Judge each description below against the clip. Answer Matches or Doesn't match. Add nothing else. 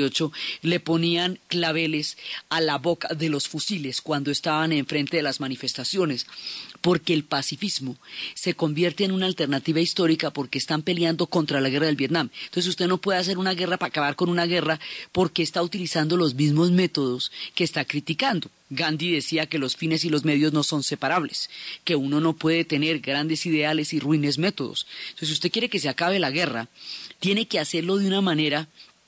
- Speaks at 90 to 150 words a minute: Doesn't match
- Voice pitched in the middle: Matches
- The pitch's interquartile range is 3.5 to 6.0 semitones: Doesn't match